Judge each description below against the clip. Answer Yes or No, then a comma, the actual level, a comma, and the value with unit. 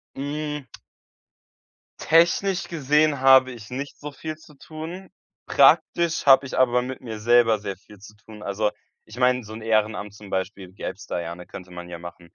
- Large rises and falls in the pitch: Yes, wide, 6.0 semitones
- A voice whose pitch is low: Yes, low, 120 Hz